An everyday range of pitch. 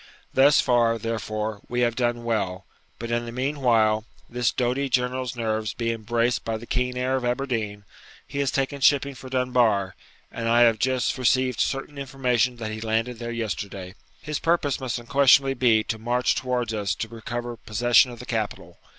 No: narrow, 2.3 semitones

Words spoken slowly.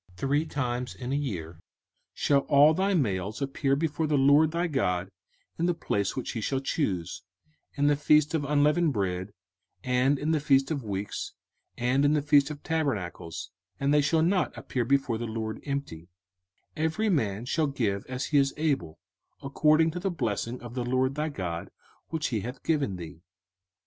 No: average, 185 wpm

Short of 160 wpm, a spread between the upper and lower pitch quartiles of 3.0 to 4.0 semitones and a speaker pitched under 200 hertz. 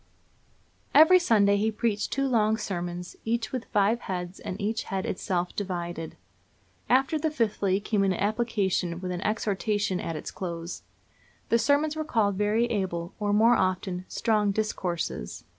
No: average, 150 wpm; average, 3.7 semitones; high, 205 Hz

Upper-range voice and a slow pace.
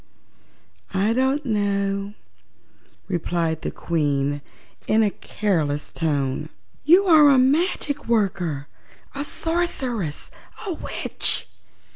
Yes: high, 205 Hz; slow, 95 wpm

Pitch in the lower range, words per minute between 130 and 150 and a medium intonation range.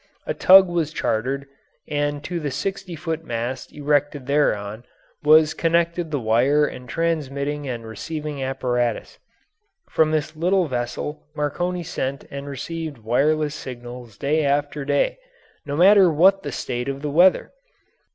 No: medium, 145 Hz; average, 140 wpm; average, 3.9 semitones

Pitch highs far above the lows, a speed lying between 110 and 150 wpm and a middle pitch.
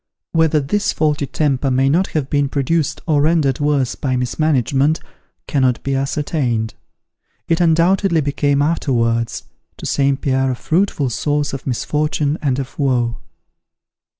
No: average, 2.8 semitones; average, 140 wpm; medium, 145 Hz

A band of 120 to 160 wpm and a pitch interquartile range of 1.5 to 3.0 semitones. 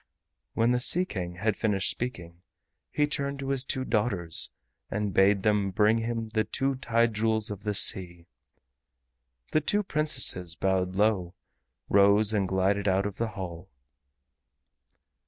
No: average, 145 wpm; average, 3.7 semitones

